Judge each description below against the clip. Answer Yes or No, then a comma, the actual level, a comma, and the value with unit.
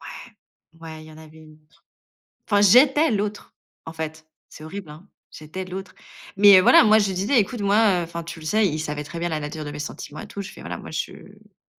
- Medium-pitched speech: Yes, medium, 170 Hz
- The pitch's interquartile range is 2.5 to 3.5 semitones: No, average, 4.5 semitones